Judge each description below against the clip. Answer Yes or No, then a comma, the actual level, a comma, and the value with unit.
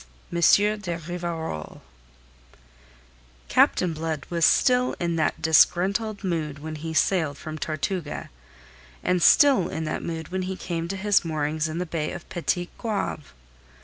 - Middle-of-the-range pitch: Yes, medium, 170 Hz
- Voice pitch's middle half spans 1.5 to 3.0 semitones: Yes, average, 2.7 semitones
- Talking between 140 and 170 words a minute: Yes, average, 145 wpm